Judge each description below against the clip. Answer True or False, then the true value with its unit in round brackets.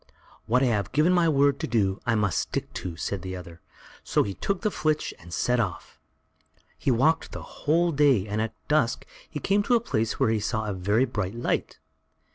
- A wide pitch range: True (6.7 semitones)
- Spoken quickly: True (210 wpm)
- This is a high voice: False (115 Hz)